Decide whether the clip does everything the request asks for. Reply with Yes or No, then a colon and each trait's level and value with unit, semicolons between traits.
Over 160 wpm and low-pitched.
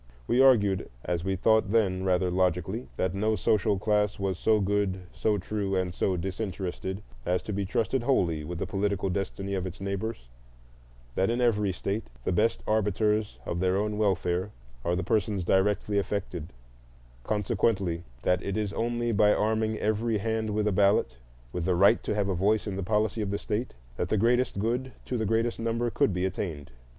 Yes: average, 180 wpm; low, 100 Hz